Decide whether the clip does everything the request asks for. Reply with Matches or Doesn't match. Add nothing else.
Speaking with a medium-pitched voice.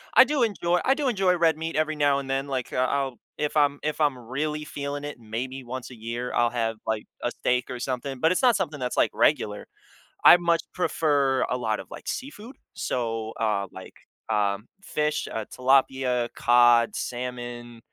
Doesn't match